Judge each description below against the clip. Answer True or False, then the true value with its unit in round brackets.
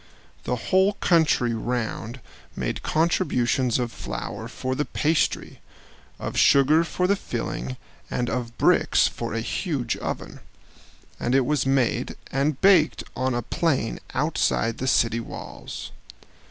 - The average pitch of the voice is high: False (130 Hz)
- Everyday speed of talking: False (130 wpm)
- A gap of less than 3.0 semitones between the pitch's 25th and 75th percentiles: False (4.7 semitones)